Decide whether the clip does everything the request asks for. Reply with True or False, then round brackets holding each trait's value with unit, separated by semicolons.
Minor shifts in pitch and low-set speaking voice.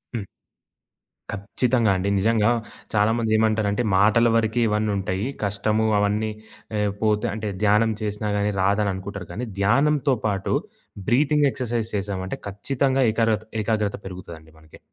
True (2.2 semitones; 105 Hz)